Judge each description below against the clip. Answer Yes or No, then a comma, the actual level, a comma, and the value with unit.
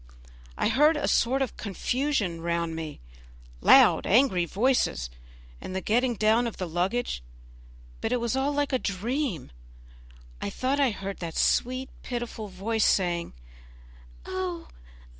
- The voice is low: No, high, 220 Hz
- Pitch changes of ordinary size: No, wide, 6.2 semitones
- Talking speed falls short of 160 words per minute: Yes, average, 140 wpm